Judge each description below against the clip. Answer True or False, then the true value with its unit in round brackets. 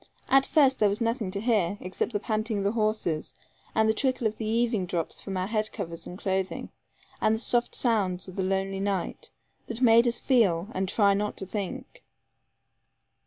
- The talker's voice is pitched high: True (210 Hz)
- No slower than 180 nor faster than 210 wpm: True (195 wpm)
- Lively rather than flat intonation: False (3.3 semitones)